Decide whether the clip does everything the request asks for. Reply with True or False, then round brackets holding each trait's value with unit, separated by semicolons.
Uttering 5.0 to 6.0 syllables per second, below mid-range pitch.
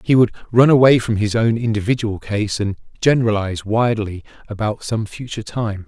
True (5.7 syllables/s; 110 Hz)